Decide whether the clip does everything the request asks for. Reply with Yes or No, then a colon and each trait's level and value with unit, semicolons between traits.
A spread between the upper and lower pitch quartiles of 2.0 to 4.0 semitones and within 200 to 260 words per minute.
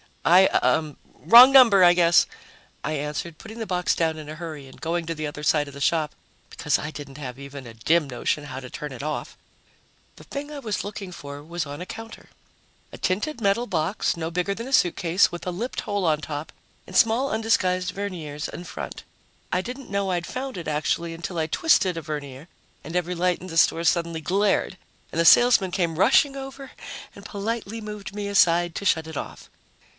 No: average, 4.6 semitones; fast, 205 wpm